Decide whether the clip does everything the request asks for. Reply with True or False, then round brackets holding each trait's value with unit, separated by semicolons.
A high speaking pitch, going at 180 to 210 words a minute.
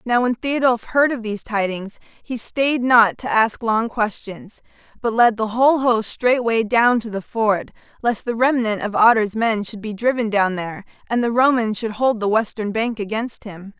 True (225 Hz; 195 wpm)